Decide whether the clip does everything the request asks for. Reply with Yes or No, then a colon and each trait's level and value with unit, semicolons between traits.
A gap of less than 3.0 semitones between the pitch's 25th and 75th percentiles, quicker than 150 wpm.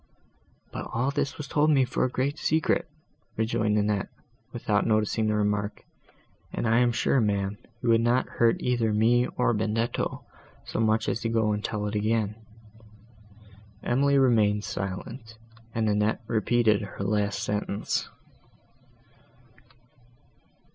No: narrow, 2.5 semitones; slow, 135 wpm